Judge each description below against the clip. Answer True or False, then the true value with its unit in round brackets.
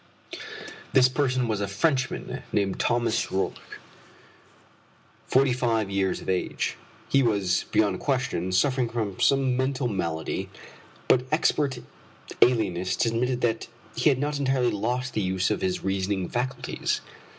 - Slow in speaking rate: True (130 wpm)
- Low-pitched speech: True (120 Hz)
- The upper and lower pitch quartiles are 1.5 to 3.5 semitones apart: False (5.0 semitones)